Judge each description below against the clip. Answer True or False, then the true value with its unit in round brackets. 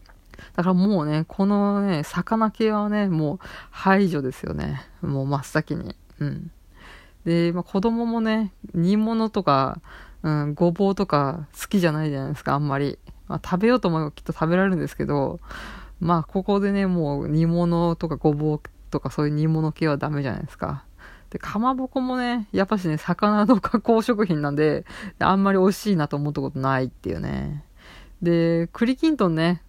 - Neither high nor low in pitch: True (170 Hz)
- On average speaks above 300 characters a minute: True (345 characters per minute)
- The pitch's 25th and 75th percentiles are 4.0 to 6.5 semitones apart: True (5.3 semitones)